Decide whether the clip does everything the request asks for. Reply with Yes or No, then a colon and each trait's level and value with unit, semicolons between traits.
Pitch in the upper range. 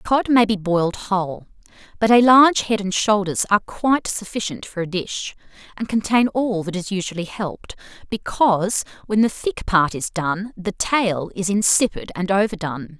Yes: high, 200 Hz